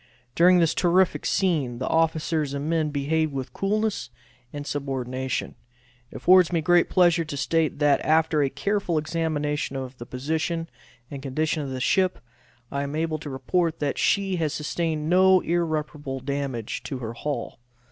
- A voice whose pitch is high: No, medium, 155 Hz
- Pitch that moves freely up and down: No, average, 3.3 semitones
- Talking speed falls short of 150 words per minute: No, average, 160 wpm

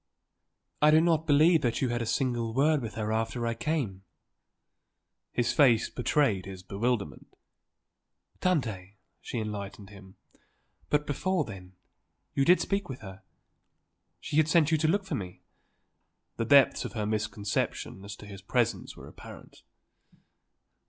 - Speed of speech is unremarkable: Yes, average, 145 wpm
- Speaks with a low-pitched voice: Yes, low, 120 Hz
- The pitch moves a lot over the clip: Yes, wide, 6.5 semitones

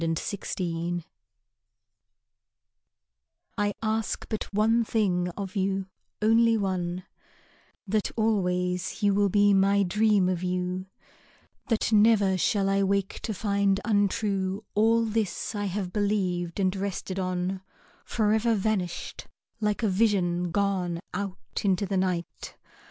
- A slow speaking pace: Yes, slow, 125 wpm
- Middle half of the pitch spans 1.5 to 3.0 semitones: Yes, narrow, 2.4 semitones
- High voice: Yes, high, 195 Hz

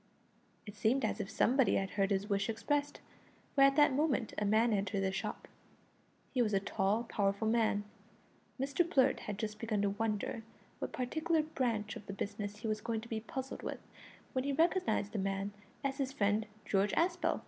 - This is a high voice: Yes, high, 220 Hz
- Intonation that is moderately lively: Yes, average, 4.7 semitones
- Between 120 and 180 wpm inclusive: No, average, 190 wpm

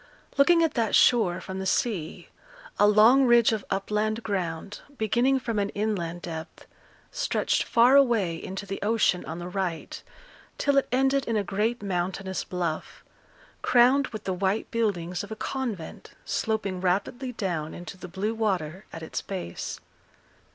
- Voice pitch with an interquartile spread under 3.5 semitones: No, average, 4.4 semitones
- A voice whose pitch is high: Yes, high, 205 Hz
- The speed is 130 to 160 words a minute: Yes, average, 155 wpm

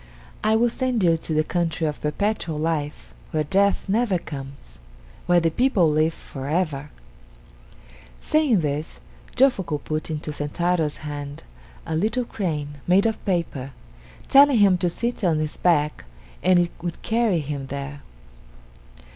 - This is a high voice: No, medium, 165 Hz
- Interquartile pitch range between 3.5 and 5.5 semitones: Yes, average, 5.2 semitones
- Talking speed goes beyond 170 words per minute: No, average, 145 wpm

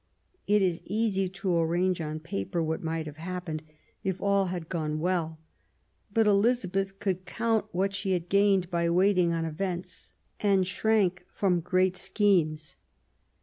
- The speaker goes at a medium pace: Yes, average, 150 wpm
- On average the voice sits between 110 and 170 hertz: No, medium, 185 Hz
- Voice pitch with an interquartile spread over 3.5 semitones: No, average, 2.8 semitones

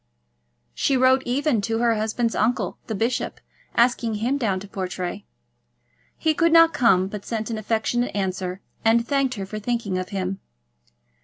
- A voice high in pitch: Yes, high, 225 Hz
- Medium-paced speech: Yes, average, 160 wpm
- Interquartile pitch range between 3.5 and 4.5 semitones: Yes, average, 3.8 semitones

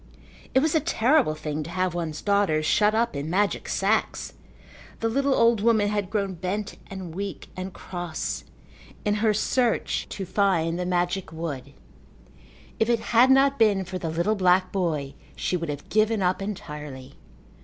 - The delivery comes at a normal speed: Yes, average, 165 wpm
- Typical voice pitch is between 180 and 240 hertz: Yes, high, 190 Hz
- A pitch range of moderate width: Yes, average, 4.4 semitones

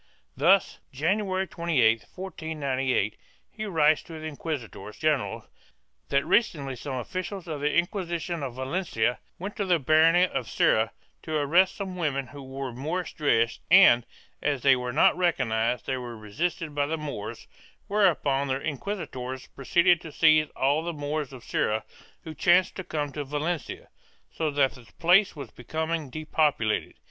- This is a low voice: No, medium, 150 Hz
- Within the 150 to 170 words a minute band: Yes, average, 155 wpm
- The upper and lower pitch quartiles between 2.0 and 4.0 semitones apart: No, average, 4.6 semitones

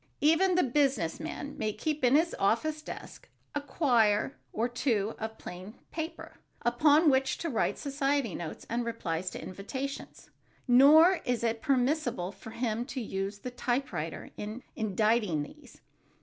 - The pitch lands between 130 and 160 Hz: No, high, 245 Hz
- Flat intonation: No, average, 5.2 semitones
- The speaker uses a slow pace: No, average, 150 wpm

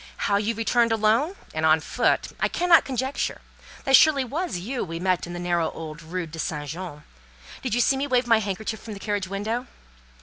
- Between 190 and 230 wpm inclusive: Yes, average, 200 wpm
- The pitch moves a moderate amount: No, wide, 6.3 semitones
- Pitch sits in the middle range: No, high, 215 Hz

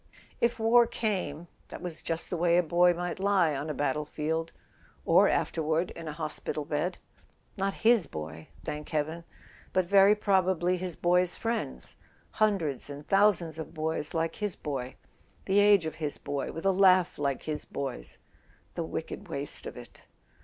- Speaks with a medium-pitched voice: Yes, medium, 170 Hz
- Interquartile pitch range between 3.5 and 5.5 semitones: Yes, average, 4.0 semitones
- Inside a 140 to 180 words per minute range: Yes, average, 165 wpm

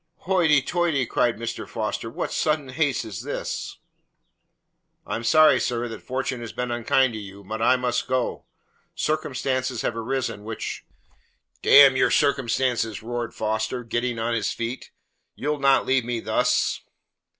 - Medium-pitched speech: No, low, 125 Hz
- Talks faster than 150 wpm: Yes, average, 160 wpm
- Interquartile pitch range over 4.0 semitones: No, average, 2.8 semitones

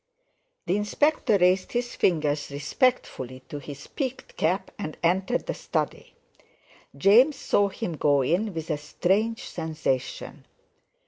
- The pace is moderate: No, slow, 125 wpm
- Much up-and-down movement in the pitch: Yes, wide, 6.2 semitones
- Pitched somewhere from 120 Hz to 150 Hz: No, medium, 180 Hz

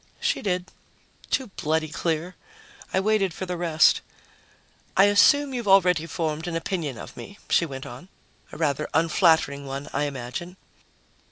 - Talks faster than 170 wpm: No, average, 150 wpm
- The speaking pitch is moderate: Yes, medium, 170 Hz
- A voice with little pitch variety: No, average, 4.0 semitones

